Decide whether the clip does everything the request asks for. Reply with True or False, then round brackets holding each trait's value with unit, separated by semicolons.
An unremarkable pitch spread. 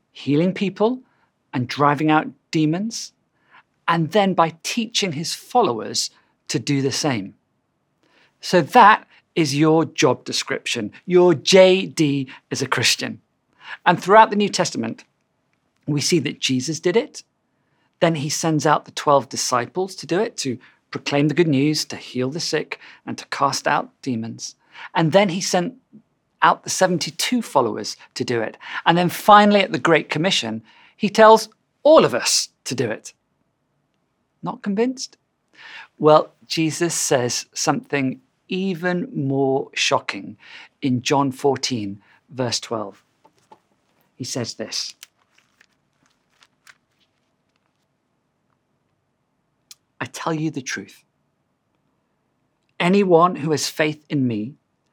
True (4.9 semitones)